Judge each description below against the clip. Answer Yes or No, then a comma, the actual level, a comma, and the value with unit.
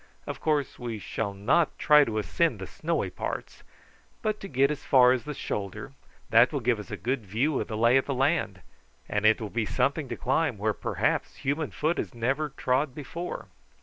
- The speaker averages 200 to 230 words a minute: Yes, fast, 205 wpm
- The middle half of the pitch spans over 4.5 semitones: Yes, average, 5.0 semitones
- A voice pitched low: Yes, low, 130 Hz